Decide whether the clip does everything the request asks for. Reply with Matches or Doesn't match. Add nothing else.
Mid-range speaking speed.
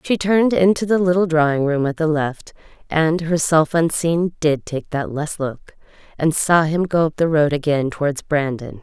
Matches